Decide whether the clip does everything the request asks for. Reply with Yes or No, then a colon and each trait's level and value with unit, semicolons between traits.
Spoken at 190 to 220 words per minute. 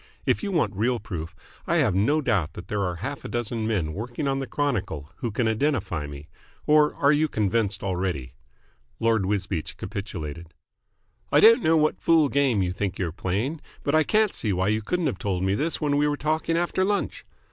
Yes: average, 200 wpm